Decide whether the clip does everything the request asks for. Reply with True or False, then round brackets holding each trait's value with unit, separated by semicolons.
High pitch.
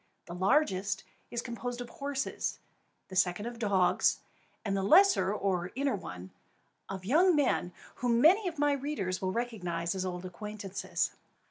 True (210 Hz)